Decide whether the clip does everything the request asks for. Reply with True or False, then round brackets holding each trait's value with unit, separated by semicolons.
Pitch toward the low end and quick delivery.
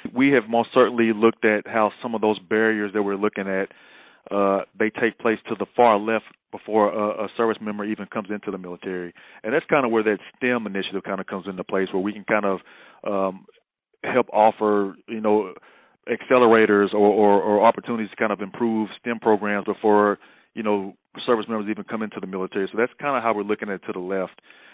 True (105 Hz; 215 wpm)